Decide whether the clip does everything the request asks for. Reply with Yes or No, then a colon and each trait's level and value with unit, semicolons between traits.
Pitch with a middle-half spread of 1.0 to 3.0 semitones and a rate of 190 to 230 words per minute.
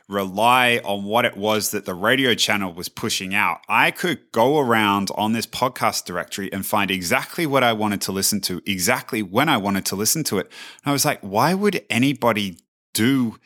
No: average, 3.5 semitones; average, 200 wpm